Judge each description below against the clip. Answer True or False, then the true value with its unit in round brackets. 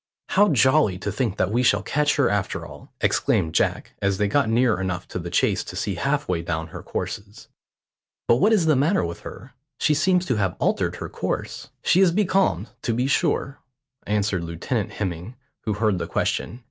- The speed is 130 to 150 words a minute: False (195 wpm)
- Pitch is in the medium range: False (110 Hz)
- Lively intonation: True (7.2 semitones)